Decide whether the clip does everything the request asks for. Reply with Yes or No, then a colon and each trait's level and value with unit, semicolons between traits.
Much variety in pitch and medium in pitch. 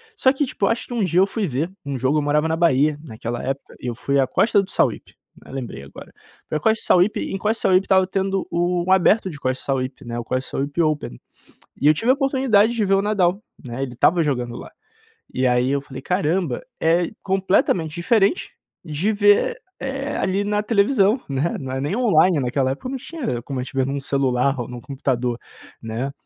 Yes: wide, 7.1 semitones; medium, 160 Hz